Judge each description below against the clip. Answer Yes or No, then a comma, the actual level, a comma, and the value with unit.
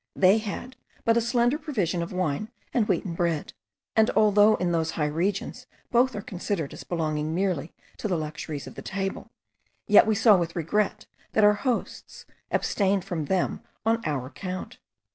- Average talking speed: Yes, average, 170 wpm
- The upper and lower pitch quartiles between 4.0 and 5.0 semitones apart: Yes, average, 4.5 semitones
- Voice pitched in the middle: No, high, 195 Hz